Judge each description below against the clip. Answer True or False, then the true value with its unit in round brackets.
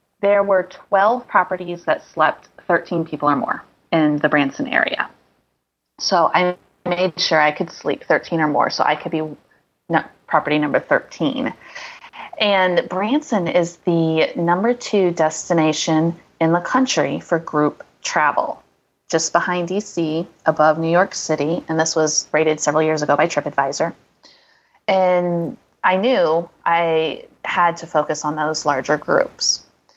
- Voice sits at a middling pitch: True (170 Hz)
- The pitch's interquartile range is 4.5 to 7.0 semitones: False (3.0 semitones)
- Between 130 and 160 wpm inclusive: True (140 wpm)